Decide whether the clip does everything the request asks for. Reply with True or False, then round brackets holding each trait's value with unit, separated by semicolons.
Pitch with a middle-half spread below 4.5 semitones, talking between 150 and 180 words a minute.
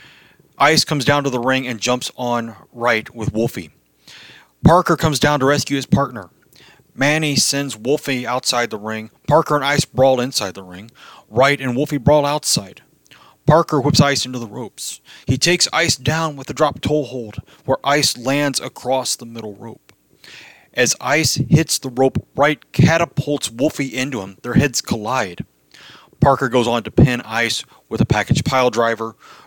True (3.3 semitones; 170 wpm)